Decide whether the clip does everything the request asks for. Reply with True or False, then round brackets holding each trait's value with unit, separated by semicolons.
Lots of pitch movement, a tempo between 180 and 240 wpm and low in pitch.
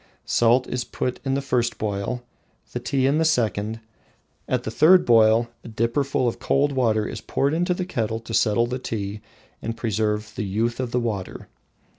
False (3.0 semitones; 185 wpm; 120 Hz)